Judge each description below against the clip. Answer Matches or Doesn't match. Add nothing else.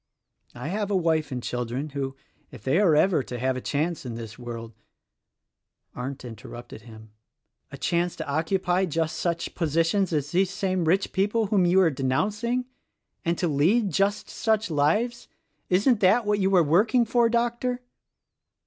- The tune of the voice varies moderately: Doesn't match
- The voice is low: Doesn't match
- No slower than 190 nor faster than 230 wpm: Doesn't match